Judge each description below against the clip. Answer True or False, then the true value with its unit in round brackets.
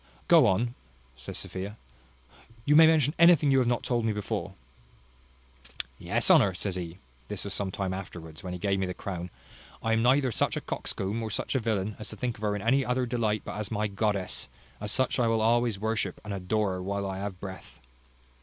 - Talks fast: True (210 wpm)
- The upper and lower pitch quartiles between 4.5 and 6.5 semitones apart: False (3.6 semitones)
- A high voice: False (105 Hz)